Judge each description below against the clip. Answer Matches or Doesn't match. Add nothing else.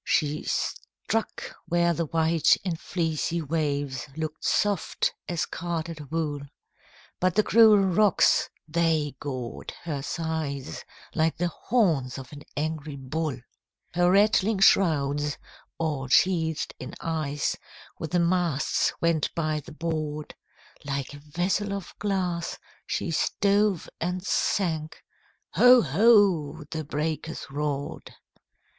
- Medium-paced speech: Doesn't match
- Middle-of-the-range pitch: Matches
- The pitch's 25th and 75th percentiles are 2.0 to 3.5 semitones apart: Matches